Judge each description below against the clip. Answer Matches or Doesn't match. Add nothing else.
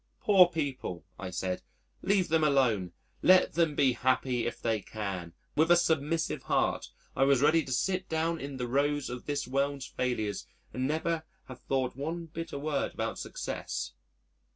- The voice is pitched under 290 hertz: Matches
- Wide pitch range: Doesn't match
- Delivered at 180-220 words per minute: Doesn't match